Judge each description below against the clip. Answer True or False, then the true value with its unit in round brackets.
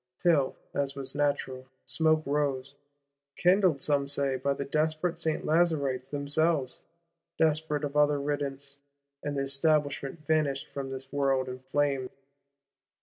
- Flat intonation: True (1.9 semitones)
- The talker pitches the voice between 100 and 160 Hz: True (140 Hz)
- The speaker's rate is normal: False (125 wpm)